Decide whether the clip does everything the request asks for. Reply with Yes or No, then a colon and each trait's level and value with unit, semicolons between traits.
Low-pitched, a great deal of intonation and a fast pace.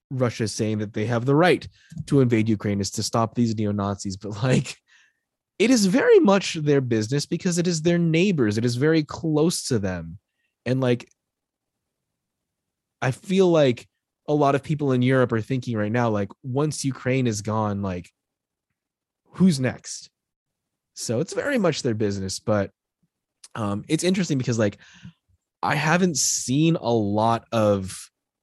No: low, 125 Hz; wide, 6.1 semitones; average, 165 wpm